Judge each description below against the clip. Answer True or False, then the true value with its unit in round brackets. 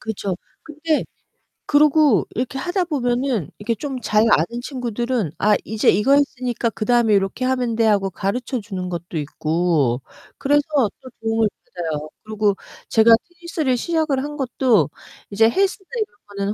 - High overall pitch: True (235 Hz)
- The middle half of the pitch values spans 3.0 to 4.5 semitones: False (5.4 semitones)